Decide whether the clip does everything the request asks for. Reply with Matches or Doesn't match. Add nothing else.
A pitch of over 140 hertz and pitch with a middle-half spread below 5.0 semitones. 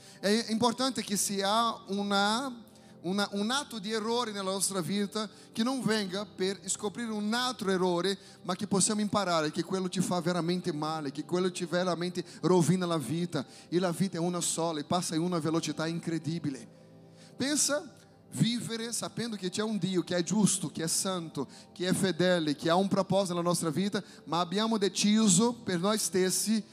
Matches